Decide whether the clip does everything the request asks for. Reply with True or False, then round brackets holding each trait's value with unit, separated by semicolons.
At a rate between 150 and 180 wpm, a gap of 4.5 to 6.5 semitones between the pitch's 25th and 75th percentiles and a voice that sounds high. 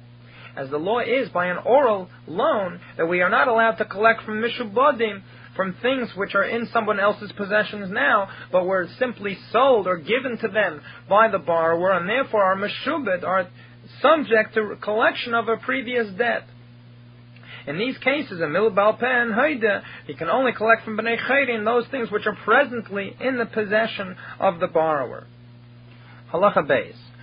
True (165 wpm; 5.0 semitones; 210 Hz)